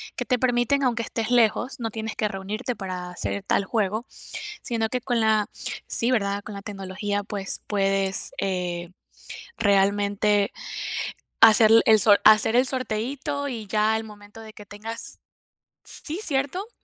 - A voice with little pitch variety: No, average, 3.0 semitones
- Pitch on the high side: Yes, high, 215 Hz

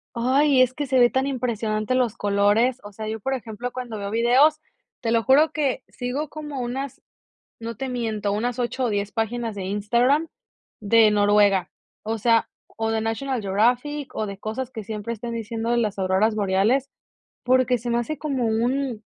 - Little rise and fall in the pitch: No, average, 3.2 semitones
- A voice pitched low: No, high, 235 Hz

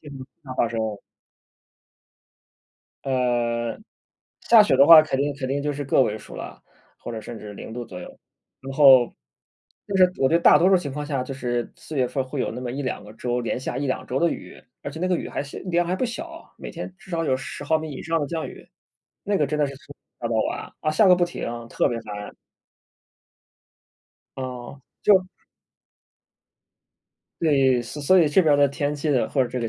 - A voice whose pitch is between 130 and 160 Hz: Yes, medium, 140 Hz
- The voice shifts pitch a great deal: No, average, 4.3 semitones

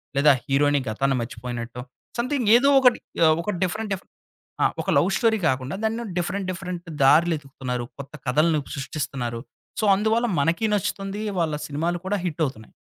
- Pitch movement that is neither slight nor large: No, wide, 6.8 semitones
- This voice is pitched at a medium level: Yes, medium, 160 Hz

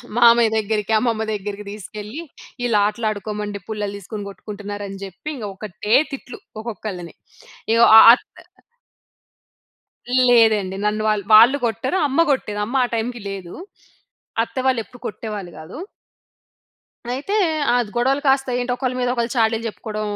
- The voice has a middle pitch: No, high, 220 Hz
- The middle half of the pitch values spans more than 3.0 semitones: No, average, 2.7 semitones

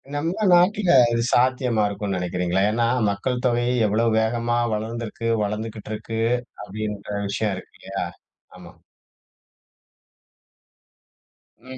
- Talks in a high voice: No, low, 110 Hz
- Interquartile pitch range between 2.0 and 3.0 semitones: Yes, average, 2.7 semitones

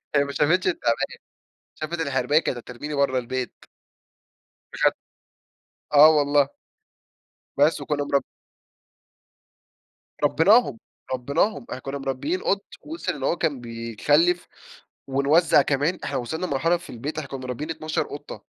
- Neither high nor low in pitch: Yes, medium, 145 Hz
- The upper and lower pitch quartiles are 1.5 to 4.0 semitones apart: Yes, average, 3.3 semitones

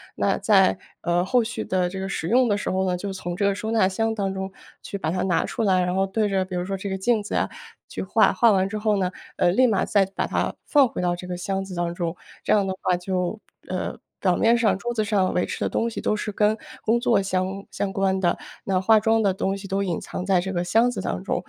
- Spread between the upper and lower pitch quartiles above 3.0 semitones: No, narrow, 2.6 semitones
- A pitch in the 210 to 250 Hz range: No, high, 195 Hz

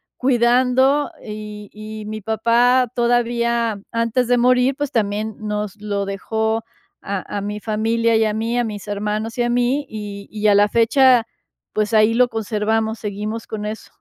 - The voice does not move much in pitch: Yes, narrow, 2.3 semitones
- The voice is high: Yes, high, 220 Hz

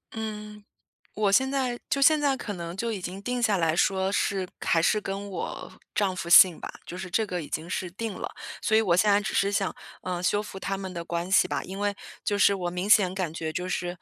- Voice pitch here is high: Yes, high, 195 Hz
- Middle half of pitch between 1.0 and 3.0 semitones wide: Yes, average, 2.7 semitones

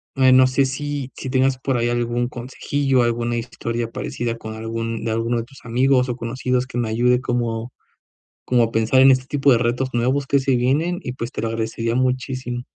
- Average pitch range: No, narrow, 2.0 semitones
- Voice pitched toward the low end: Yes, low, 125 Hz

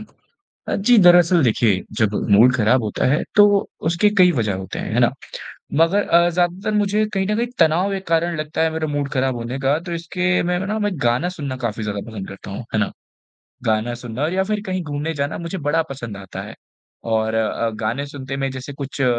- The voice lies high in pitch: No, medium, 145 Hz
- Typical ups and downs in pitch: No, wide, 7.2 semitones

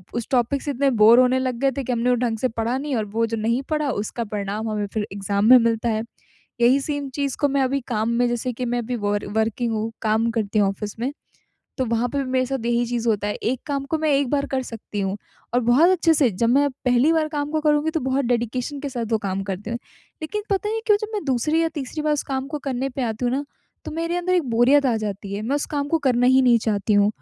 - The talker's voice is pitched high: Yes, high, 245 Hz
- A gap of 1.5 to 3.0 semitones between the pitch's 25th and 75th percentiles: No, average, 3.9 semitones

